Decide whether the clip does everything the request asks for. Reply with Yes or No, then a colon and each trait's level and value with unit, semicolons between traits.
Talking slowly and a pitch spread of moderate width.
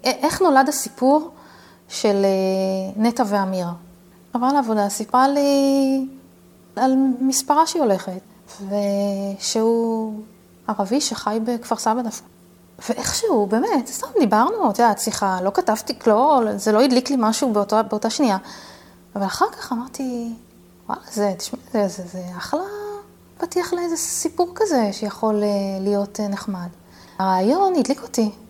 No: average, 125 wpm; average, 5.0 semitones